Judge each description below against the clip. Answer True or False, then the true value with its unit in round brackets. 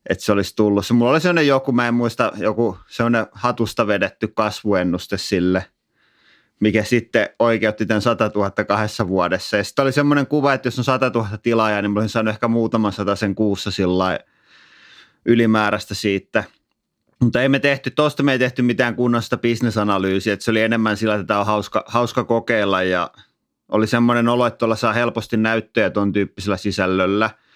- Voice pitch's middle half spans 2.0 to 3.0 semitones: True (2.7 semitones)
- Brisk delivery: True (180 wpm)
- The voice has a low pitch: True (110 Hz)